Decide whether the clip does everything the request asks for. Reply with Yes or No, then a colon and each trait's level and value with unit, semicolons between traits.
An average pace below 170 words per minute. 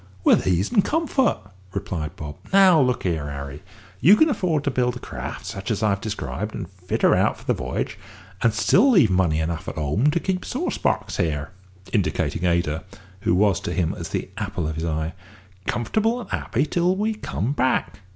No: average, 200 wpm